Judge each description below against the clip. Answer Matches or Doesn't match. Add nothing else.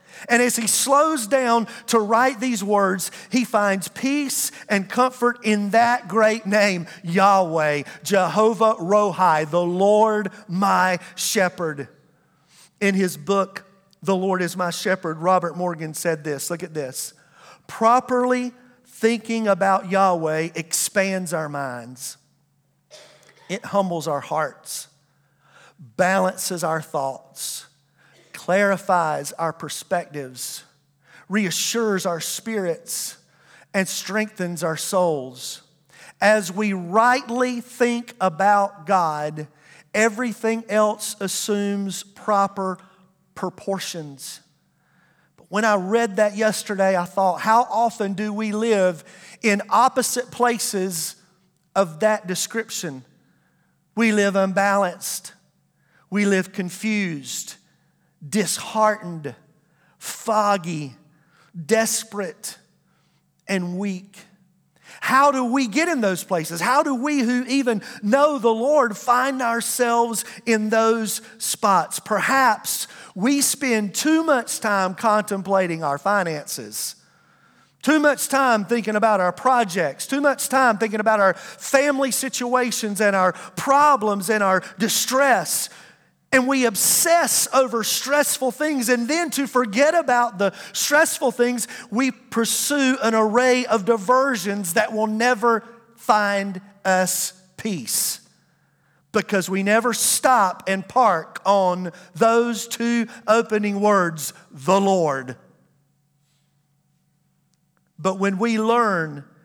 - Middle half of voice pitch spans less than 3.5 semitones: Doesn't match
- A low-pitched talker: Doesn't match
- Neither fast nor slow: Doesn't match